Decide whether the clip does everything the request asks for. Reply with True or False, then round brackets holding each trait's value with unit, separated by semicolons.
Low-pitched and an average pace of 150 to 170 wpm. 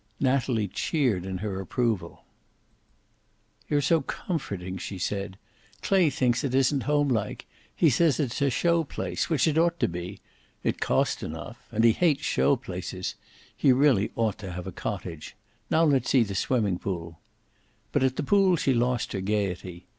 True (120 Hz; 165 wpm)